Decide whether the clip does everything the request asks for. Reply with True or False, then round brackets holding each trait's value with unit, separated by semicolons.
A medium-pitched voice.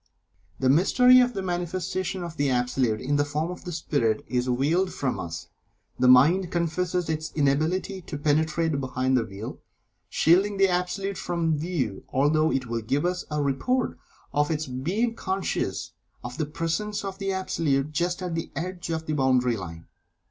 True (160 Hz)